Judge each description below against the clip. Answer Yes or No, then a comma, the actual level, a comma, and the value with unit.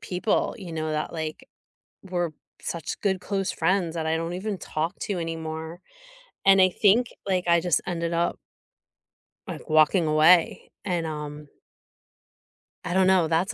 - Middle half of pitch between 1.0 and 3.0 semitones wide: Yes, average, 2.7 semitones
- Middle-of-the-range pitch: Yes, medium, 170 Hz